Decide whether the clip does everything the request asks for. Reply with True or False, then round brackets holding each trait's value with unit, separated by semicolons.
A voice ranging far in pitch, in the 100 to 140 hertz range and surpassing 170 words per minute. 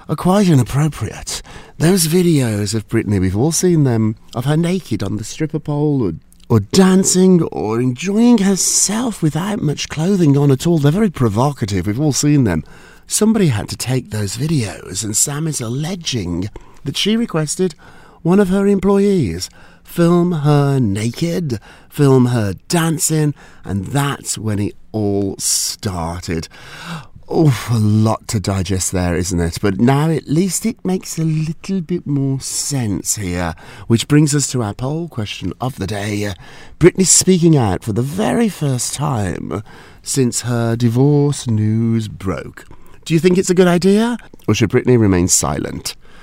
False (7.8 semitones; 135 Hz; 155 wpm)